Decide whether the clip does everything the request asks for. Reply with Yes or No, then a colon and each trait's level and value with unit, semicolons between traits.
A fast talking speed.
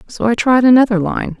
Yes: fast, 215 wpm